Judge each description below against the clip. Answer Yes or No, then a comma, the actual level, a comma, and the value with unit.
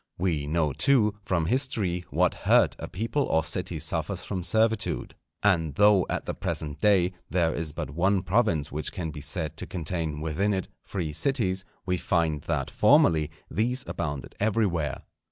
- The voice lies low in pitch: Yes, very low, 90 Hz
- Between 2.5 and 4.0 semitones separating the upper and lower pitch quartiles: No, average, 4.5 semitones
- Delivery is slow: No, average, 165 wpm